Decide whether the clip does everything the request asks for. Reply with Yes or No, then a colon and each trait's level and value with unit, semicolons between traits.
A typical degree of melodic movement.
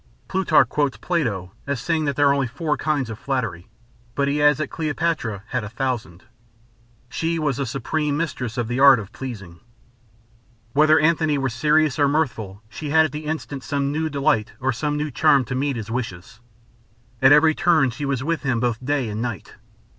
Yes: average, 4.3 semitones